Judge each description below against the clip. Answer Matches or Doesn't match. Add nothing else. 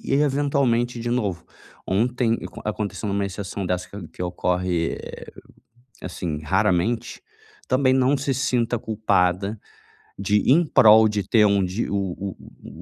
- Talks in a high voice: Doesn't match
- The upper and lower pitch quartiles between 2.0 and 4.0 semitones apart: Doesn't match